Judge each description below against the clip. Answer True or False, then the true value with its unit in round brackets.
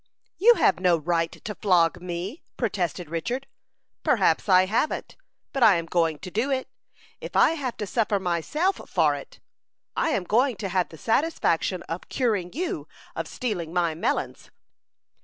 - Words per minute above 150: True (160 wpm)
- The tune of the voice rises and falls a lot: True (6.4 semitones)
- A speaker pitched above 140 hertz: True (190 Hz)